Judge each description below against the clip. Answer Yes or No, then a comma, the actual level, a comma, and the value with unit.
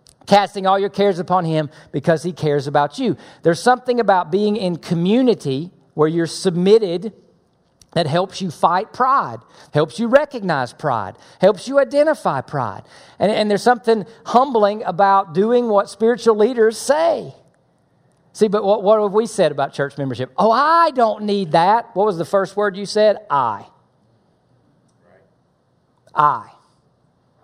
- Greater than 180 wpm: No, average, 150 wpm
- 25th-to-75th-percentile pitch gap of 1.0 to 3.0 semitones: No, average, 5.0 semitones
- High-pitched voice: Yes, high, 195 Hz